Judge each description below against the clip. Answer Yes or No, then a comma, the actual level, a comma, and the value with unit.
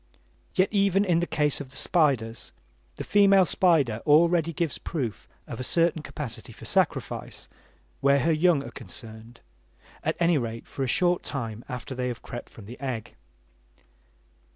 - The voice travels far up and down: Yes, wide, 6.0 semitones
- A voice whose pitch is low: No, medium, 145 Hz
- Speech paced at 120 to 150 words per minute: No, average, 160 wpm